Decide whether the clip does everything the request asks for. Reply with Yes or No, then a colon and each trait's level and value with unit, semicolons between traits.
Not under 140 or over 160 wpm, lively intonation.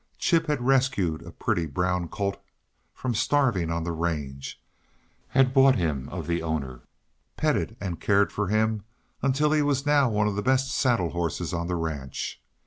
No: average, 170 wpm; wide, 7.9 semitones